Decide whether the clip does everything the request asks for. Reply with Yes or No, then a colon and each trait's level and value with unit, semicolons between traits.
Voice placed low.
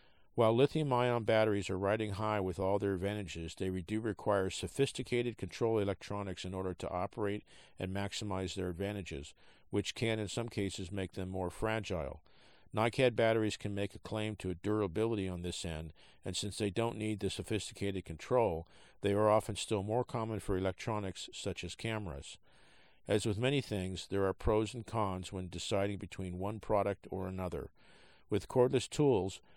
Yes: low, 100 Hz